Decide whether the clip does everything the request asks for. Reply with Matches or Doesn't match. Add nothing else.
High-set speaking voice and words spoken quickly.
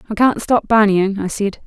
Matches